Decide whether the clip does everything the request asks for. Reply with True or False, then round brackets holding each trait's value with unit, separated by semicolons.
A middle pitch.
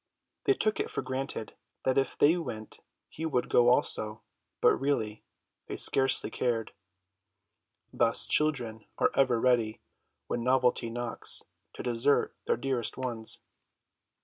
False (125 Hz)